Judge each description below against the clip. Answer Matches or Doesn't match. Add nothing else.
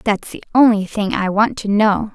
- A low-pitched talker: Doesn't match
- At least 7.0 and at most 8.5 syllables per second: Doesn't match